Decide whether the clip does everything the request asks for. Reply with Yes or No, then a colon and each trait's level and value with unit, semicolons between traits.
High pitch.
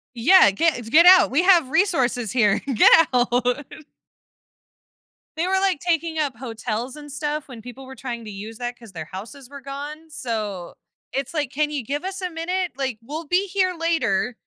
Yes: very high, 275 Hz